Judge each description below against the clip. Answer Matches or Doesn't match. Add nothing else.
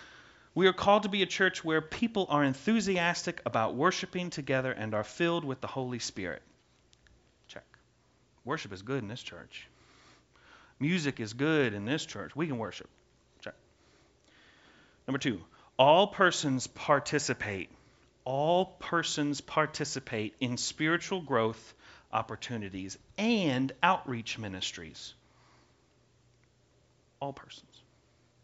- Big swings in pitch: Matches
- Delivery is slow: Matches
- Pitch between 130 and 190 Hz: Matches